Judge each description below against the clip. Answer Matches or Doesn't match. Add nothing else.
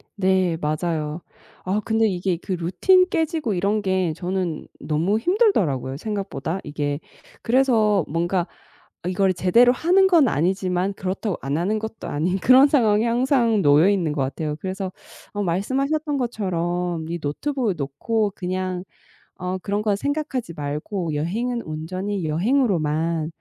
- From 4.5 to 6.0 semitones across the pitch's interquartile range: Matches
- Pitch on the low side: Doesn't match